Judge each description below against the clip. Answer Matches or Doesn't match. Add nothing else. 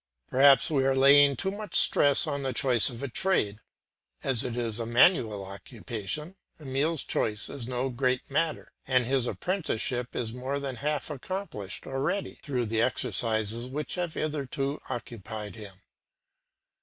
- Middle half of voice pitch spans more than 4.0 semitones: Doesn't match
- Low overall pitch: Matches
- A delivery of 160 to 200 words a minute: Doesn't match